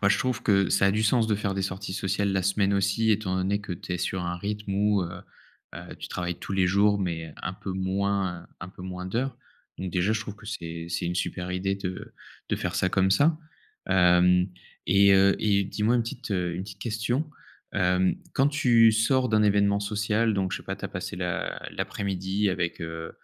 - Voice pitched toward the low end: Yes, low, 100 Hz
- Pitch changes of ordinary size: No, narrow, 2.3 semitones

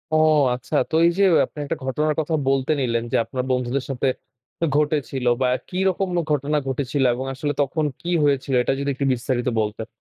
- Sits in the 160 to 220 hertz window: No, low, 135 Hz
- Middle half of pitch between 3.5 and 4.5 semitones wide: No, average, 2.9 semitones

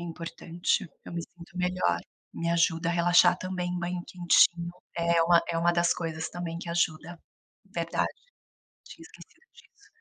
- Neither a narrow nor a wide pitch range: No, narrow, 0.9 semitones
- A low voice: No, medium, 170 Hz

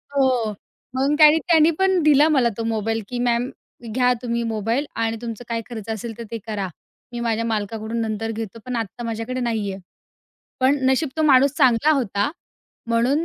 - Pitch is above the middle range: Yes, high, 235 Hz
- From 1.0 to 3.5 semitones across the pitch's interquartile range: Yes, average, 3.0 semitones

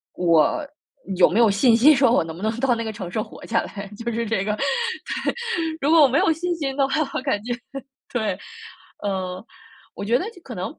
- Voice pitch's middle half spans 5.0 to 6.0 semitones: Yes, wide, 5.4 semitones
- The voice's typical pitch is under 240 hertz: Yes, high, 230 Hz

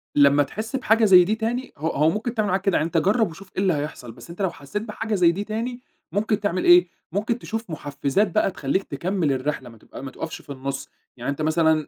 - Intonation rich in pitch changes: Yes, wide, 6.4 semitones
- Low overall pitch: No, medium, 180 Hz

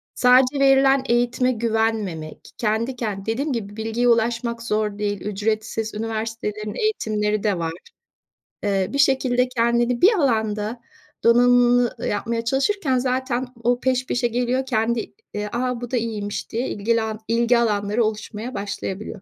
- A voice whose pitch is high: Yes, high, 230 Hz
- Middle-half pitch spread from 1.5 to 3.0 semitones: Yes, average, 2.7 semitones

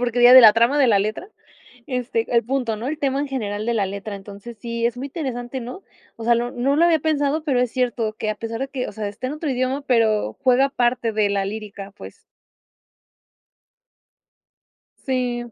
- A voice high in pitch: Yes, high, 240 Hz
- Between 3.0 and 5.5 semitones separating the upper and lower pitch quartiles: Yes, average, 3.4 semitones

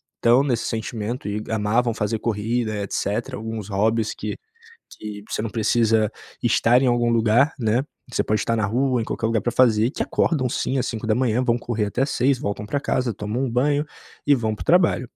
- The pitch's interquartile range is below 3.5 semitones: Yes, narrow, 2.5 semitones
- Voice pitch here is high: No, low, 115 Hz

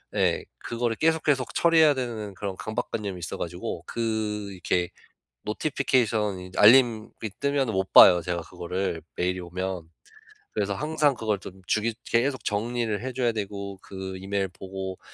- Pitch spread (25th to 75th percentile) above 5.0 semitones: No, average, 4.2 semitones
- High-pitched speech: No, low, 105 Hz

